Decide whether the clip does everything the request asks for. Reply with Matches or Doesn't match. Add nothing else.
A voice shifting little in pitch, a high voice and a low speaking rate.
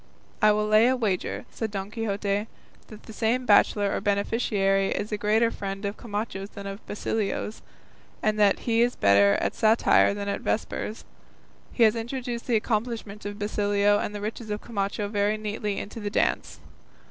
Doesn't match